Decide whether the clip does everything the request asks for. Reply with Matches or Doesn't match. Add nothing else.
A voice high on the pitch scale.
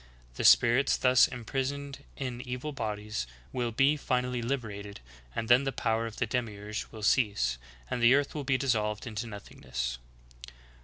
Doesn't match